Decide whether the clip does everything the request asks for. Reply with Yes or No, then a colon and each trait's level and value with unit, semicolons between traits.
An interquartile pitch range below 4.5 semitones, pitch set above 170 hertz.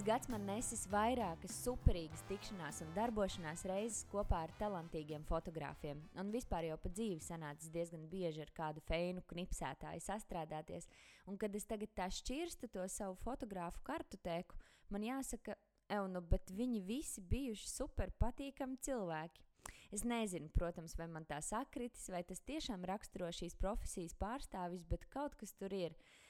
No: average, 5.0 semitones; high, 190 Hz